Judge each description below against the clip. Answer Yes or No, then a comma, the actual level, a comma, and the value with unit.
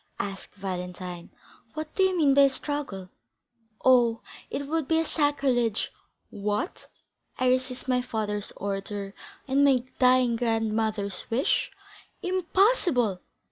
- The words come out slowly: Yes, slow, 120 wpm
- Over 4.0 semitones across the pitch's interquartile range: Yes, wide, 5.6 semitones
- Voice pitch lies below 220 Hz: No, high, 245 Hz